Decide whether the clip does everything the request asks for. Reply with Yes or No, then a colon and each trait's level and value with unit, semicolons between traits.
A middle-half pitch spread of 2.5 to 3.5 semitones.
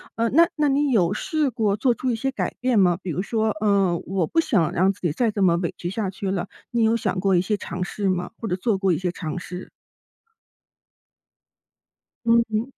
No: average, 4.2 semitones